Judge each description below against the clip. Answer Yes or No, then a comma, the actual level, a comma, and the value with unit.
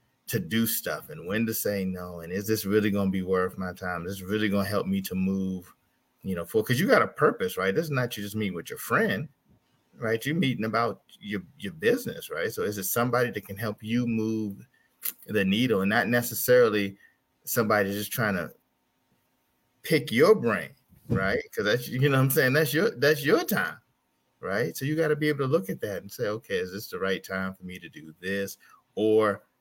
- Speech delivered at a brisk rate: Yes, fast, 225 wpm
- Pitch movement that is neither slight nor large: Yes, average, 4.4 semitones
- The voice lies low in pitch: Yes, low, 110 Hz